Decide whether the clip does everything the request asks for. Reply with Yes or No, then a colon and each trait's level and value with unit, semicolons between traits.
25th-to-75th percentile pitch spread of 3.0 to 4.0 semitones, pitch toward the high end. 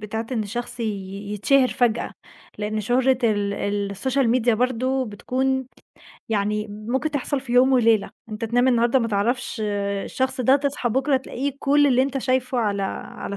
Yes: average, 3.5 semitones; high, 245 Hz